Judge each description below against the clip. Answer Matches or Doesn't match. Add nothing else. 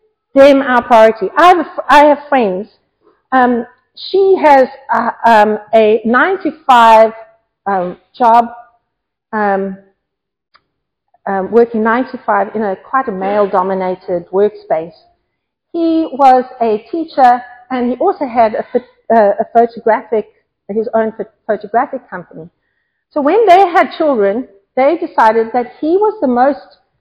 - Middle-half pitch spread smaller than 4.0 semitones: Doesn't match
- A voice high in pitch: Matches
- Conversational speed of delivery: Doesn't match